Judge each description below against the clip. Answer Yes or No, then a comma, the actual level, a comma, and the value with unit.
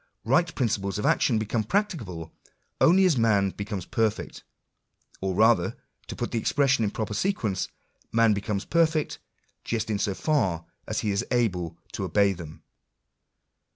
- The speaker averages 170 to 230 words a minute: No, average, 155 wpm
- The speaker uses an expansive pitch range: No, average, 3.8 semitones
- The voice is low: Yes, low, 110 Hz